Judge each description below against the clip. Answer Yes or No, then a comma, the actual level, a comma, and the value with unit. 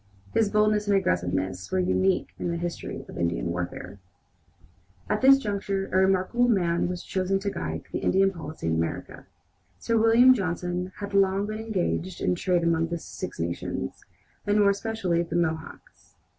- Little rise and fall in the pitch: No, average, 3.6 semitones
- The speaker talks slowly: No, average, 165 wpm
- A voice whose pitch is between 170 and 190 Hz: Yes, medium, 185 Hz